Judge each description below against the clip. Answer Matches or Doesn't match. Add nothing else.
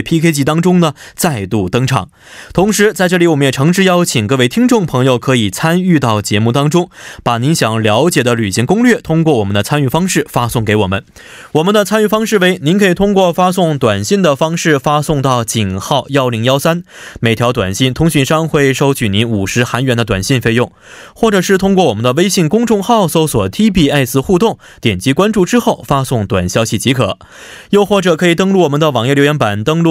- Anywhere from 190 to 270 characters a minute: Doesn't match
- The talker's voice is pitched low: Doesn't match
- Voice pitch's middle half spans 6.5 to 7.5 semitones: Matches